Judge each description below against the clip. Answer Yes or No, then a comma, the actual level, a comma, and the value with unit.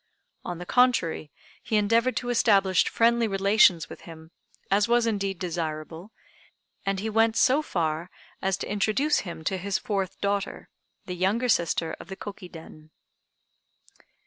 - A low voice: No, high, 195 Hz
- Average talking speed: Yes, average, 145 wpm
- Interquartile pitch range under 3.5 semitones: No, average, 4.4 semitones